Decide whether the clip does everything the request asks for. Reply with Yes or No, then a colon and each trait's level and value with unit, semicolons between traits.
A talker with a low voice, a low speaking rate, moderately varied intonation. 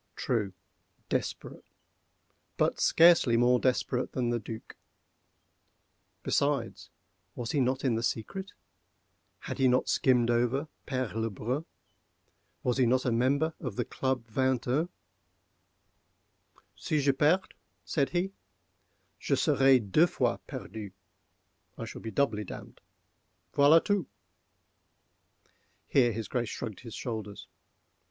Yes: low, 125 Hz; slow, 110 wpm; average, 3.6 semitones